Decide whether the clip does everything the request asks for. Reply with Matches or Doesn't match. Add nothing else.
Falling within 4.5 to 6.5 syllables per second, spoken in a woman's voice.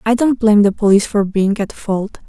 Matches